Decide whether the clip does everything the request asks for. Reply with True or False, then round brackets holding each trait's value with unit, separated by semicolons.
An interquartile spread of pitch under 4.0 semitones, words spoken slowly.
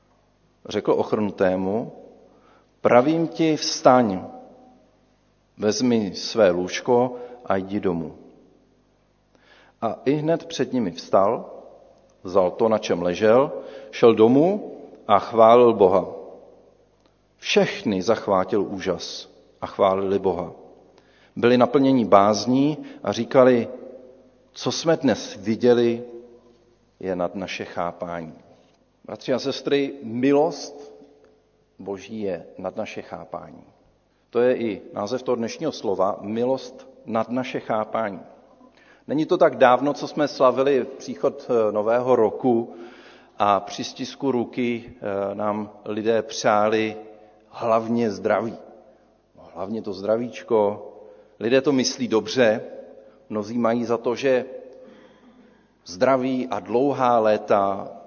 False (4.4 semitones; 105 wpm)